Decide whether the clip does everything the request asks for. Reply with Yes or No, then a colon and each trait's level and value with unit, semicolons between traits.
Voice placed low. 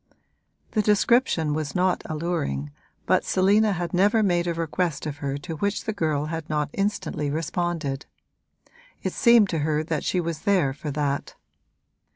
No: medium, 165 Hz